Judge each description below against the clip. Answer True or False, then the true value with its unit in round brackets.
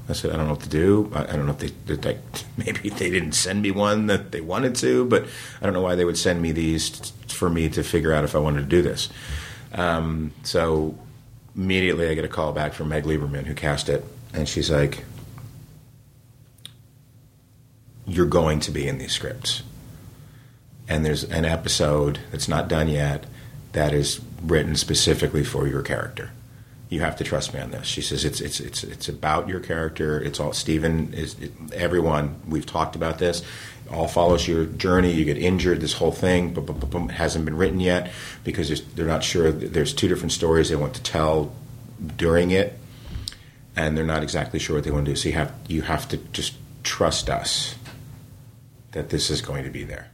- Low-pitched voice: True (85 Hz)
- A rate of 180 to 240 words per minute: True (200 wpm)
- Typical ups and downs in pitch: False (7.5 semitones)